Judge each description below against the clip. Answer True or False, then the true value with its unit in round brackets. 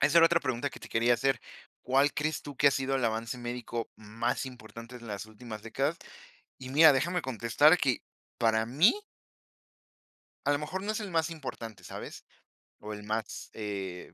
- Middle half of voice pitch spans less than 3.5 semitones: False (4.4 semitones)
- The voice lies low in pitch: True (125 Hz)